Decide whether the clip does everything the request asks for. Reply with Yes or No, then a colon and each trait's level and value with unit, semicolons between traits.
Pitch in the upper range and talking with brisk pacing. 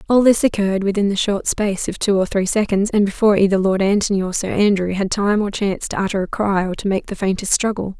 Yes: high, 200 Hz; fast, 255 wpm